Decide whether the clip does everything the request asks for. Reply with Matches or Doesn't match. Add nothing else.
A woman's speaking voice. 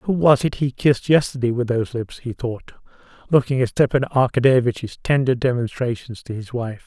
Doesn't match